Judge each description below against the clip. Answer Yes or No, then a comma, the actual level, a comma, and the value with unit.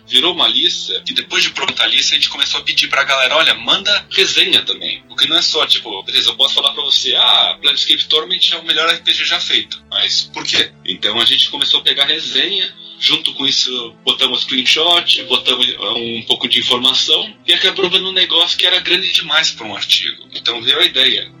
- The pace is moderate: No, fast, 215 wpm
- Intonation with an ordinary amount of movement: No, wide, 6.6 semitones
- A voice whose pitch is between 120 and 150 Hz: Yes, low, 135 Hz